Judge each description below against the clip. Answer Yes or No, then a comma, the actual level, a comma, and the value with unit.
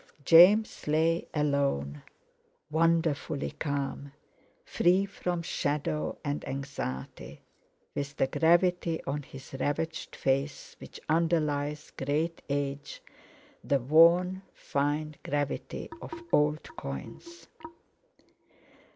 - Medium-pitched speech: Yes, medium, 150 Hz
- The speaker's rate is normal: No, slow, 90 wpm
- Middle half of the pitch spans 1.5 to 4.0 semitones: Yes, average, 2.9 semitones